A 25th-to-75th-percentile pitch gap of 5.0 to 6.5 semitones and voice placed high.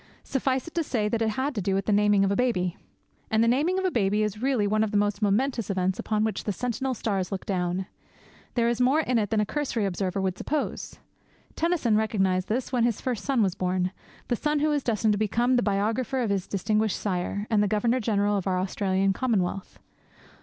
No: average, 4.1 semitones; high, 215 Hz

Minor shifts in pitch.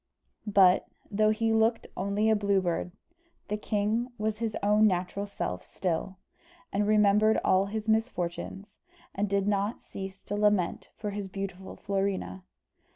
Yes: narrow, 1.9 semitones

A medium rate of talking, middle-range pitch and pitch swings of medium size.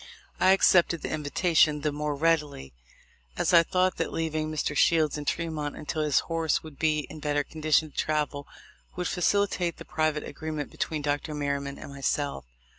No: average, 180 wpm; medium, 155 Hz; narrow, 2.0 semitones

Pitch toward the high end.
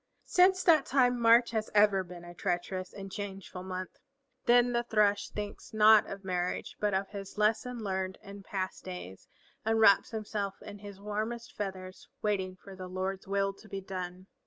Yes: high, 200 Hz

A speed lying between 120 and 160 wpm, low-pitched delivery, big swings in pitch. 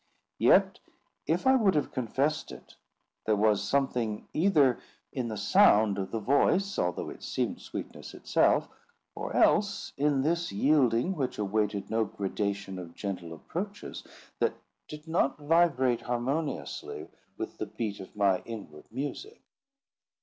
Yes: slow, 135 wpm; low, 120 Hz; wide, 6.8 semitones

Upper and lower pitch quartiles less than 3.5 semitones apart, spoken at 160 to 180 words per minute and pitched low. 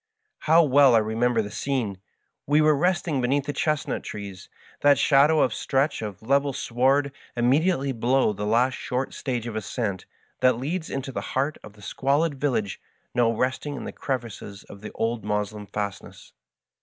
No: average, 4.5 semitones; average, 170 wpm; low, 130 Hz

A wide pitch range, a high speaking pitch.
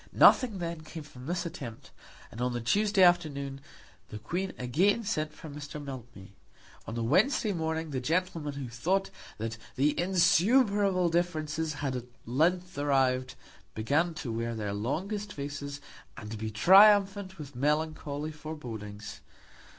No: wide, 5.9 semitones; medium, 150 Hz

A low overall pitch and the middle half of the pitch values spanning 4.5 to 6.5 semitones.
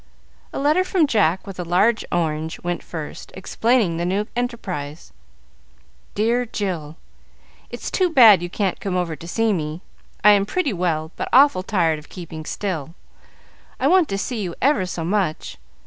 No: medium, 185 Hz; wide, 5.5 semitones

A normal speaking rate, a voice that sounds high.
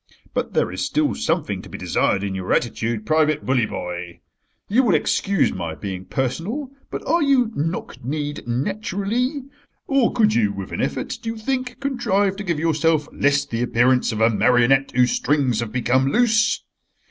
No: average, 175 wpm; medium, 145 Hz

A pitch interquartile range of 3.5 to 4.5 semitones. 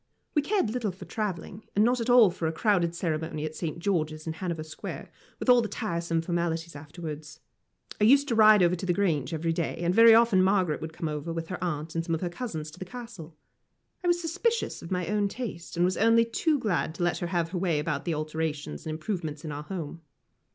No: average, 4.9 semitones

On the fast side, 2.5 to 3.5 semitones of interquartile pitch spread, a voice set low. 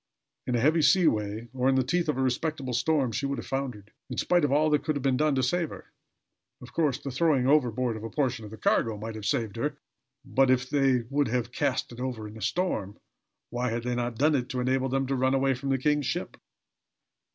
Yes: fast, 240 wpm; average, 3.0 semitones; low, 130 Hz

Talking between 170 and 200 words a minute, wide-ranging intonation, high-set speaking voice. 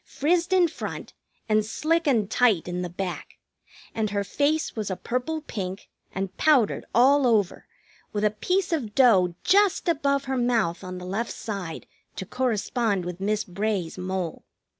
No: average, 160 wpm; wide, 6.7 semitones; high, 215 Hz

